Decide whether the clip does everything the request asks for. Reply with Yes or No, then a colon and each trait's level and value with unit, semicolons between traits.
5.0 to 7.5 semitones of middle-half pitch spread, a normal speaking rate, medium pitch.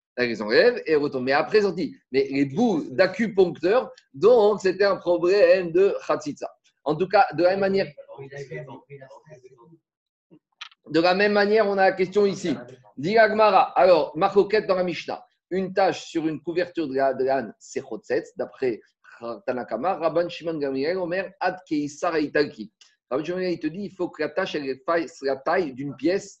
Yes: wide, 5.4 semitones; average, 175 wpm; medium, 180 Hz